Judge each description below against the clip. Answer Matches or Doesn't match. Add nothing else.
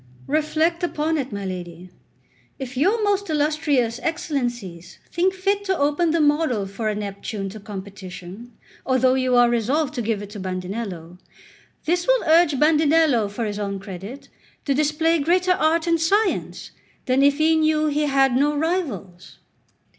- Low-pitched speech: Doesn't match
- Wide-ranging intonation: Matches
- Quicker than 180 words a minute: Doesn't match